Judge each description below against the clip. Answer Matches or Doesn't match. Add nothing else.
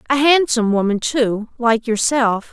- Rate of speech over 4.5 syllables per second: Doesn't match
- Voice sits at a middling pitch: Doesn't match